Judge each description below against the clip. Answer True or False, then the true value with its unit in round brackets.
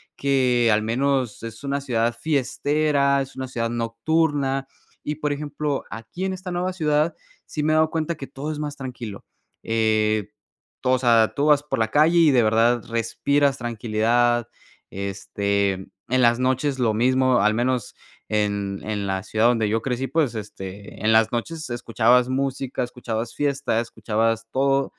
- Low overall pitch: True (125 Hz)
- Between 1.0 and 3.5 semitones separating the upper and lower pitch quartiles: False (4.0 semitones)